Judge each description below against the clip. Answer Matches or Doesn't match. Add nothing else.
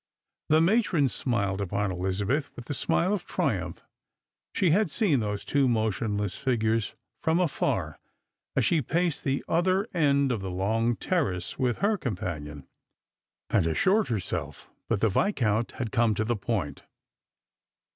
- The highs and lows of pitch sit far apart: Matches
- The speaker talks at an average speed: Matches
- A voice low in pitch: Matches